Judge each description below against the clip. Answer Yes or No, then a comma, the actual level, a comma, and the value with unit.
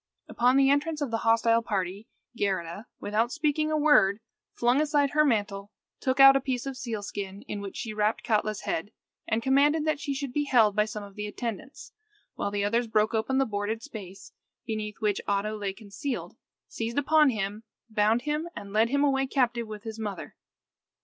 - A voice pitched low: No, high, 225 Hz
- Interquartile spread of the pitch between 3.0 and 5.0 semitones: Yes, average, 4.6 semitones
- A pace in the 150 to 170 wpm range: No, average, 190 wpm